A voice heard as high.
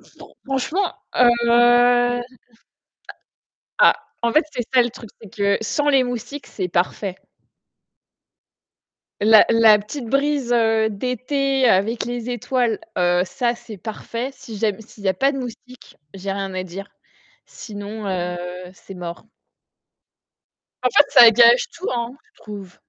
Yes: high, 230 Hz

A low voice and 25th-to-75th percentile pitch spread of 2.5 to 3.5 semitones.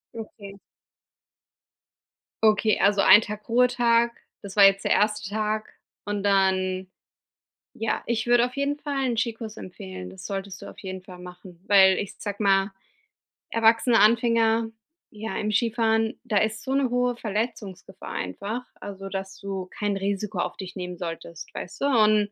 No: high, 210 Hz; average, 2.9 semitones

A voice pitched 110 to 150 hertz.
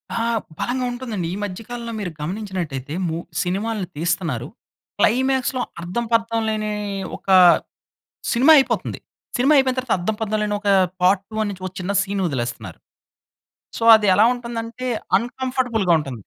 No: high, 215 Hz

